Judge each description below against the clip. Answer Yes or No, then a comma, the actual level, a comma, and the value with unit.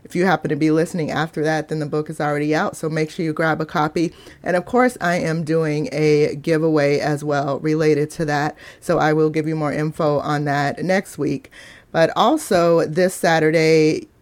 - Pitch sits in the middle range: Yes, medium, 155 Hz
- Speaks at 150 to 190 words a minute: No, fast, 205 wpm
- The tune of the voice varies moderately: No, narrow, 1.6 semitones